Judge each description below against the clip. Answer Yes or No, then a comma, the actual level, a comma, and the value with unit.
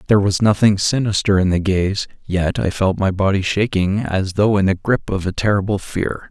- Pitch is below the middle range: Yes, low, 100 Hz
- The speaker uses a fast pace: Yes, fast, 210 wpm